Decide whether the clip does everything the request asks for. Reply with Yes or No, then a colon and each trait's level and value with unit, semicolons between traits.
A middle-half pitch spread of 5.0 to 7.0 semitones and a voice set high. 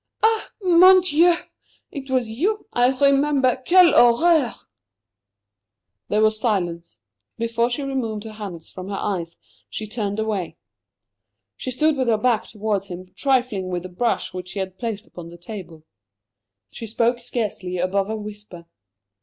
Yes: average, 5.3 semitones; high, 220 Hz